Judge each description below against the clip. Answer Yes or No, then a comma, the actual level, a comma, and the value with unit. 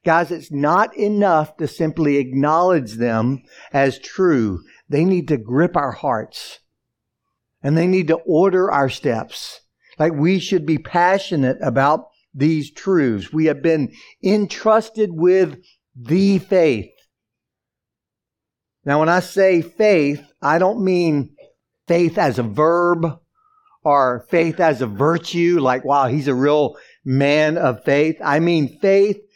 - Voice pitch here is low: No, medium, 160 Hz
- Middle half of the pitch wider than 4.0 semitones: Yes, average, 4.4 semitones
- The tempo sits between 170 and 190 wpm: No, slow, 135 wpm